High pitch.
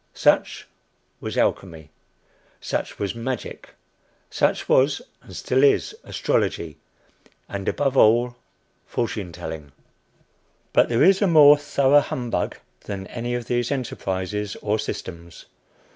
No: low, 115 Hz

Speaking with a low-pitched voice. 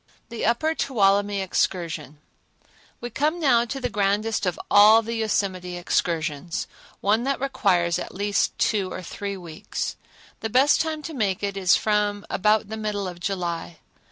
No: high, 205 Hz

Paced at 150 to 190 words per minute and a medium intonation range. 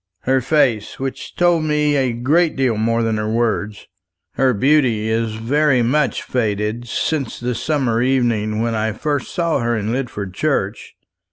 Yes: average, 160 wpm; average, 4.2 semitones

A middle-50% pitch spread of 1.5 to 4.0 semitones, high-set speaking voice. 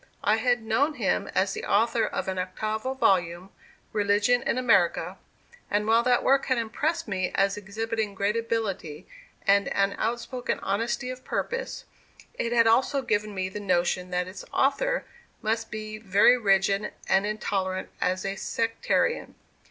Yes: average, 3.3 semitones; high, 215 Hz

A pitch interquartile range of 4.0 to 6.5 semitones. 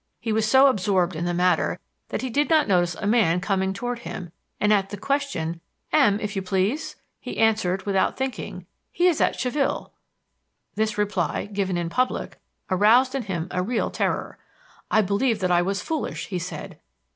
Yes: average, 5.0 semitones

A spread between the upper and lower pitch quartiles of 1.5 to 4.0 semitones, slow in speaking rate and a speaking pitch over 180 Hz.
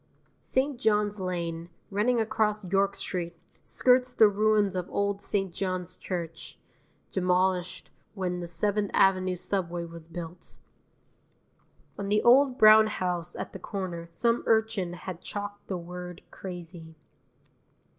Yes: average, 3.1 semitones; slow, 125 wpm; high, 190 Hz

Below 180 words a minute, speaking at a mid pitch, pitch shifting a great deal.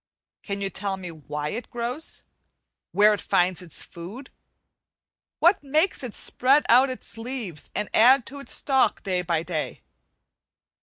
No: average, 150 wpm; high, 215 Hz; wide, 6.6 semitones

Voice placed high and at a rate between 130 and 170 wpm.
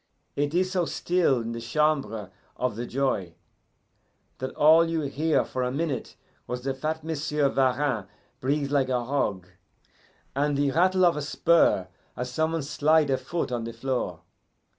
No: medium, 140 Hz; average, 165 wpm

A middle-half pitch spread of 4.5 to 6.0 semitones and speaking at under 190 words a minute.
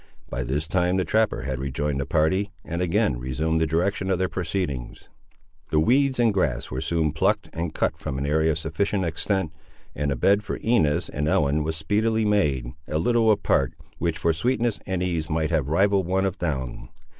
No: average, 5.0 semitones; average, 195 wpm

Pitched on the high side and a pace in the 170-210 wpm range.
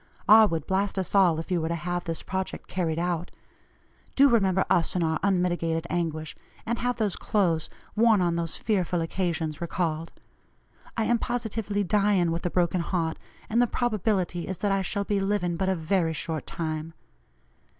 No: medium, 180 Hz; average, 180 wpm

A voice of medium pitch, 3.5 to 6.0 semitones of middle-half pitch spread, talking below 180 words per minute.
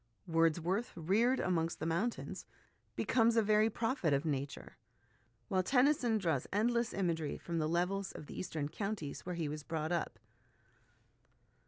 Yes: medium, 180 Hz; average, 5.3 semitones; average, 145 wpm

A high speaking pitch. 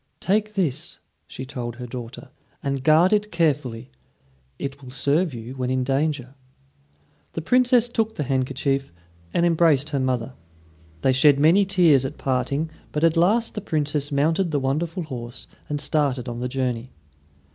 No: medium, 140 Hz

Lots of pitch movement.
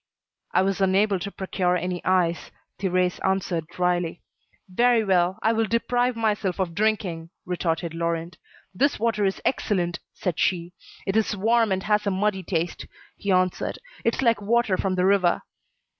No: average, 3.0 semitones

